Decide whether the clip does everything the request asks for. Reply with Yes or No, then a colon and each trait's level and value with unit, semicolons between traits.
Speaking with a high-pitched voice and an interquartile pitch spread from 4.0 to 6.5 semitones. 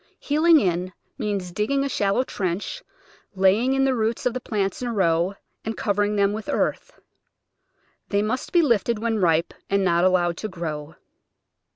Yes: high, 205 Hz; average, 4.6 semitones